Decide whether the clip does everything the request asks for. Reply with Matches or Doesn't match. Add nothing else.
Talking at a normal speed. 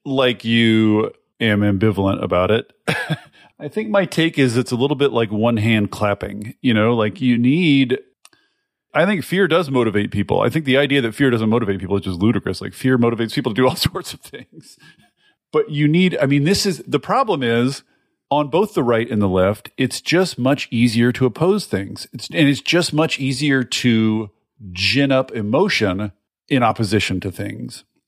Matches